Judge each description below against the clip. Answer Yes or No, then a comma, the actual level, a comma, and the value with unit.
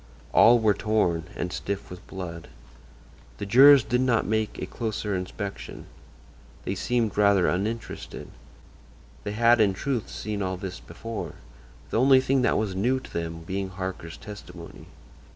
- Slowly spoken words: No, average, 150 wpm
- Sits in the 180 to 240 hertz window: No, low, 105 Hz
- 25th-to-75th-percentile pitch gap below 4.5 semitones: Yes, average, 3.8 semitones